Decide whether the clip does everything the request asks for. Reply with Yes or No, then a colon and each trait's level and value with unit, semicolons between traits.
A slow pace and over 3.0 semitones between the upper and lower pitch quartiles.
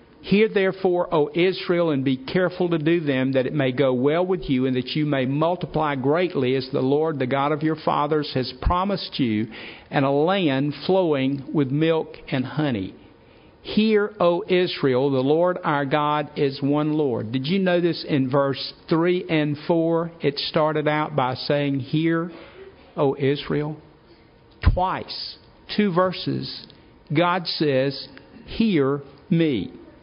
No: average, 150 wpm; average, 4.0 semitones